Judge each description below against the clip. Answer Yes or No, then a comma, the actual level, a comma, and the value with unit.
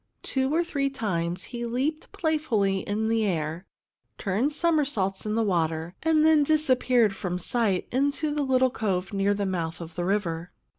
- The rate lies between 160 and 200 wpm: Yes, average, 165 wpm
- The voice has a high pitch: Yes, high, 220 Hz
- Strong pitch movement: Yes, wide, 7.1 semitones